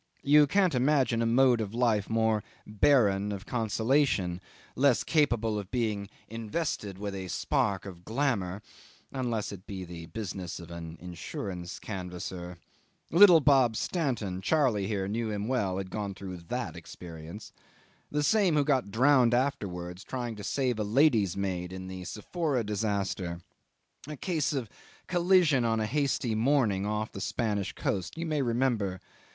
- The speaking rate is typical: Yes, average, 150 wpm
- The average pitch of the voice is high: No, low, 110 Hz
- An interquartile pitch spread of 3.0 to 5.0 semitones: No, wide, 5.6 semitones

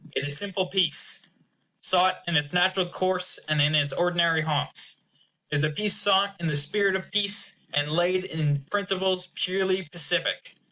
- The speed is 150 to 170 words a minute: Yes, average, 160 wpm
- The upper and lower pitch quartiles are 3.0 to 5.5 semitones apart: Yes, average, 3.8 semitones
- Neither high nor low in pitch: Yes, medium, 180 Hz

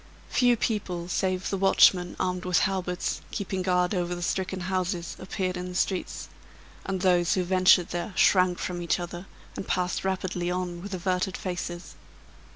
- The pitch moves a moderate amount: No, narrow, 1.2 semitones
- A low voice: No, medium, 180 Hz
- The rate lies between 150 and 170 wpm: Yes, average, 160 wpm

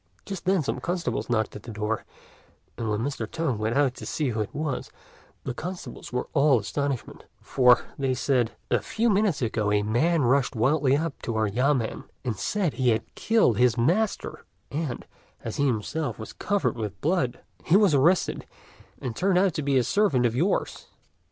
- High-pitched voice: No, low, 130 Hz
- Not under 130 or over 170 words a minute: No, average, 185 wpm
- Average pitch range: No, wide, 6.0 semitones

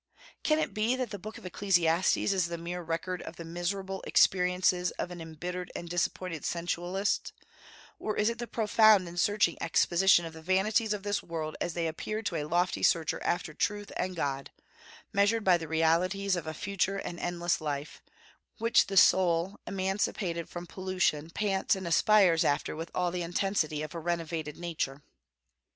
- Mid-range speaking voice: Yes, medium, 175 Hz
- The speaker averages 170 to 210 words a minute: Yes, average, 175 wpm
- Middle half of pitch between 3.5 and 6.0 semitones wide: No, average, 2.8 semitones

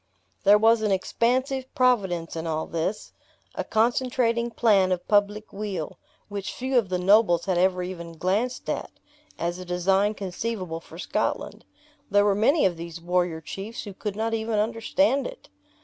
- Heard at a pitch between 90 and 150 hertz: No, high, 205 Hz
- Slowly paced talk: No, average, 165 wpm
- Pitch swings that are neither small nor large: Yes, average, 4.2 semitones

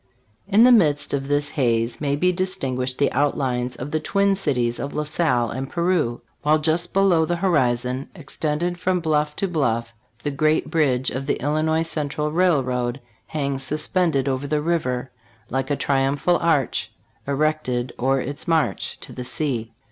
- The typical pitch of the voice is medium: Yes, medium, 145 Hz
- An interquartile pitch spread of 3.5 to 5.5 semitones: Yes, average, 3.8 semitones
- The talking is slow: No, average, 170 wpm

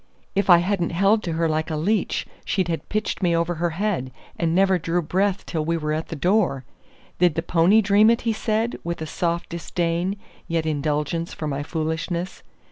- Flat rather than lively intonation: No, average, 3.2 semitones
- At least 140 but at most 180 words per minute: No, average, 200 wpm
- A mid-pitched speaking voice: Yes, medium, 170 Hz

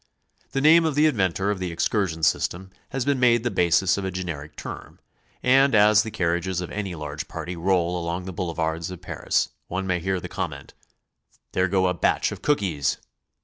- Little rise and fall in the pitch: No, average, 3.7 semitones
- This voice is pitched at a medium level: No, very low, 95 Hz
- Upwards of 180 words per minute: Yes, average, 200 wpm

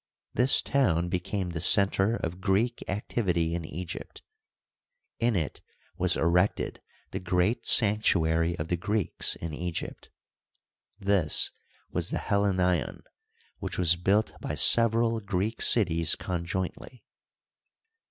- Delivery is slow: Yes, slow, 115 wpm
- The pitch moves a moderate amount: Yes, average, 3.7 semitones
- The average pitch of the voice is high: No, very low, 90 Hz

